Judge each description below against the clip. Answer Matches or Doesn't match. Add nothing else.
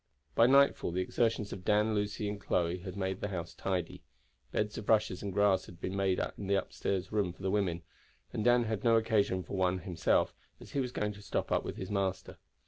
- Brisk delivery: Matches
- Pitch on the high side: Doesn't match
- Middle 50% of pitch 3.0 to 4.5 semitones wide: Doesn't match